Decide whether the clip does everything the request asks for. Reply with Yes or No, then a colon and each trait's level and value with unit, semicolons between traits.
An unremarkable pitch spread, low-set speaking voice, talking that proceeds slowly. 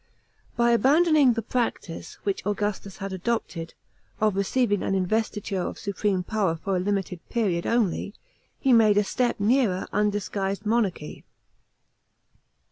No: average, 3.3 semitones; high, 205 Hz; slow, 125 wpm